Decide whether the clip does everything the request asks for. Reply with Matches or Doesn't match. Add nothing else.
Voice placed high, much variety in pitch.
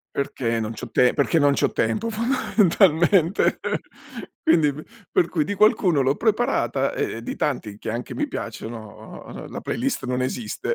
Doesn't match